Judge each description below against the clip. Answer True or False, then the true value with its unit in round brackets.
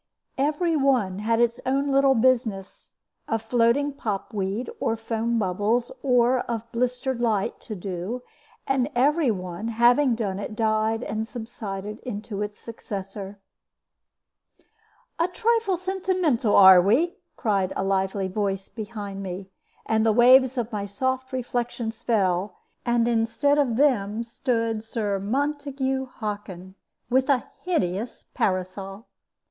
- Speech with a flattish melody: False (4.3 semitones)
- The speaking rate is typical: False (130 wpm)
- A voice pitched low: False (230 Hz)